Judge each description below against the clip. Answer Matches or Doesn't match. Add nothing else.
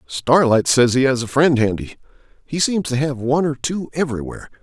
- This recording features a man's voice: Matches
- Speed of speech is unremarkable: Matches